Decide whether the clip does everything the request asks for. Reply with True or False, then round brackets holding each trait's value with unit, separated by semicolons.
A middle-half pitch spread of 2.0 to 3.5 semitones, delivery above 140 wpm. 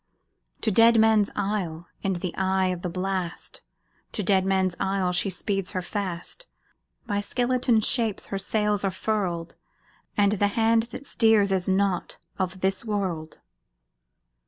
False (2.5 semitones; 135 wpm)